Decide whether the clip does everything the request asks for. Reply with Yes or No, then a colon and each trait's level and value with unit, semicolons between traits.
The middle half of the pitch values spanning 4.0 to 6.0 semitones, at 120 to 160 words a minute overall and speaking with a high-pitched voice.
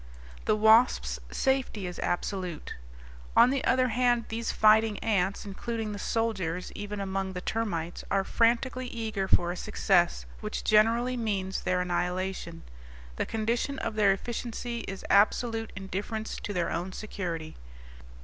No: average, 3.5 semitones; average, 140 wpm; high, 210 Hz